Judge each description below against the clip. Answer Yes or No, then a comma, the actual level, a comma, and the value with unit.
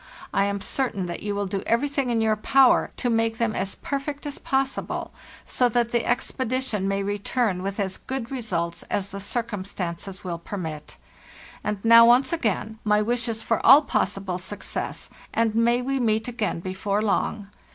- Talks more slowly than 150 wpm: No, average, 170 wpm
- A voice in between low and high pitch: No, high, 220 Hz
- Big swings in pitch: No, average, 3.6 semitones